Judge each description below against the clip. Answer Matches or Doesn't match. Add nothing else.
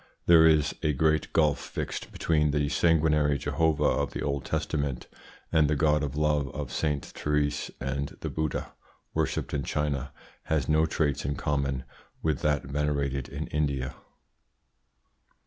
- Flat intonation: Matches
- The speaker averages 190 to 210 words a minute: Doesn't match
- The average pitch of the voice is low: Matches